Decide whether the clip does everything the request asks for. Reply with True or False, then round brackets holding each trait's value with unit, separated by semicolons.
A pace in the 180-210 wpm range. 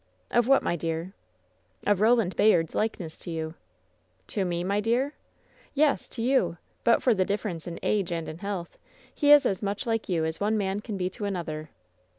True (195 wpm)